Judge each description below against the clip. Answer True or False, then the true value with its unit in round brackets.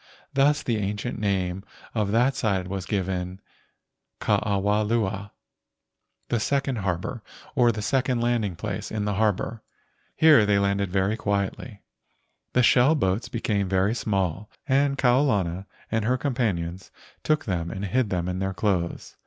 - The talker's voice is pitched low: True (105 Hz)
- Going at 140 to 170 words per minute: True (155 wpm)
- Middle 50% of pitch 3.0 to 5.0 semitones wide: True (3.9 semitones)